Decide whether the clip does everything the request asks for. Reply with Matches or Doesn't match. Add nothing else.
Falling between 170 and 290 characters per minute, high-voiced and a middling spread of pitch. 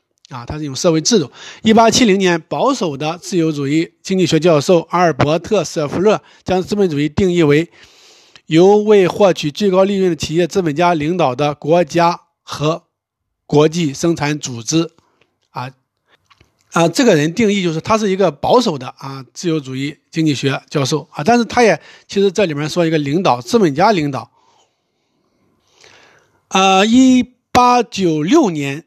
Doesn't match